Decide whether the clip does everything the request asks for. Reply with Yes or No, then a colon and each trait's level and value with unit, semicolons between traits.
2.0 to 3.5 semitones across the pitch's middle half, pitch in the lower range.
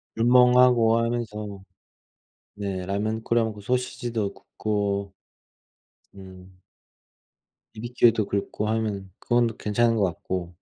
Yes: average, 3.0 semitones; low, 110 Hz